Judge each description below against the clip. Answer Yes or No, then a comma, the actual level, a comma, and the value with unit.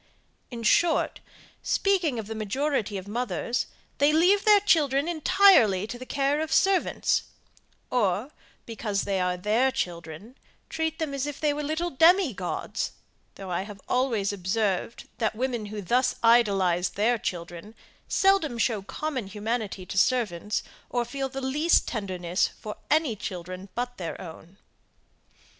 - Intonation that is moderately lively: No, wide, 6.5 semitones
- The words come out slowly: No, average, 150 wpm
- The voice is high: Yes, high, 230 Hz